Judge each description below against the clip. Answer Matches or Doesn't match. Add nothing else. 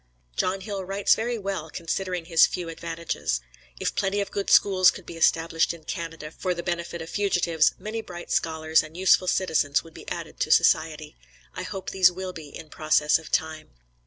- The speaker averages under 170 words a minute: Doesn't match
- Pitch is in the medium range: Matches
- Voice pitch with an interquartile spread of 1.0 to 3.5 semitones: Matches